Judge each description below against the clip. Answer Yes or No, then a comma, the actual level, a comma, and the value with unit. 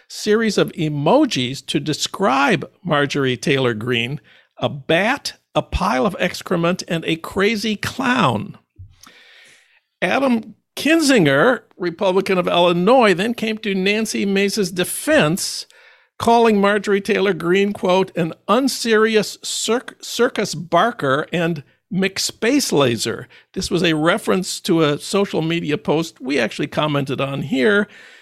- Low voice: No, high, 190 Hz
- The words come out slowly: Yes, slow, 120 wpm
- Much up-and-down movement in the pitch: Yes, wide, 5.7 semitones